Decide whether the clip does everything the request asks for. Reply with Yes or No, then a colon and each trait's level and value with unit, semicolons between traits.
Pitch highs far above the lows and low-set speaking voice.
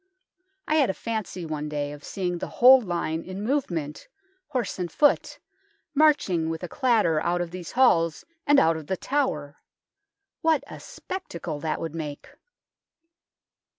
No: wide, 8.1 semitones; medium, 175 Hz